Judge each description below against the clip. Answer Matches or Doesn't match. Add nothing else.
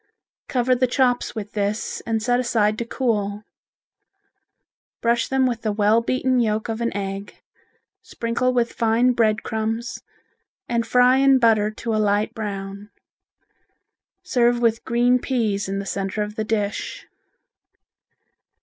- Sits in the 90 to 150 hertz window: Doesn't match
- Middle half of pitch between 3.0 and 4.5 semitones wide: Doesn't match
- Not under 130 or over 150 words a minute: Matches